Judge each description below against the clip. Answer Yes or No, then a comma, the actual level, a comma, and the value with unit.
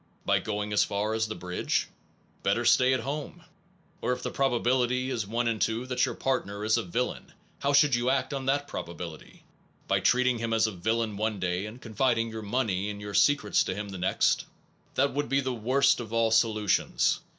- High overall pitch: No, low, 115 Hz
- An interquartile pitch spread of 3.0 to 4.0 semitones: Yes, average, 3.5 semitones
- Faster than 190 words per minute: Yes, average, 200 wpm